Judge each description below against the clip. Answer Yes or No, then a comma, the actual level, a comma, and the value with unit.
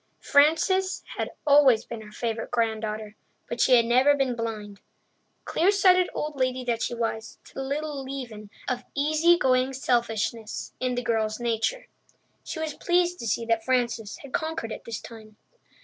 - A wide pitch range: No, average, 4.4 semitones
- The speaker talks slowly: No, average, 165 wpm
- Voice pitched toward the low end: No, high, 245 Hz